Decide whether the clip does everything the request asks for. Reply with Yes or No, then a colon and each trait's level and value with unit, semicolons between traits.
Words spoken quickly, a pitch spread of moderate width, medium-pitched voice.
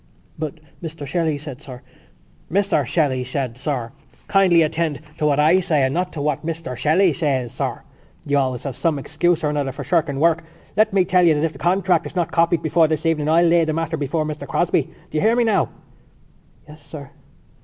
Yes: fast, 210 wpm; average, 3.0 semitones; medium, 155 Hz